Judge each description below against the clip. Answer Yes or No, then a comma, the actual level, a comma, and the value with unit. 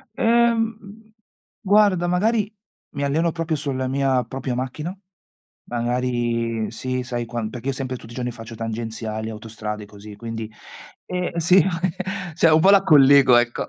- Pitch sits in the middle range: No, low, 130 Hz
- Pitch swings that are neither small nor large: No, wide, 6.7 semitones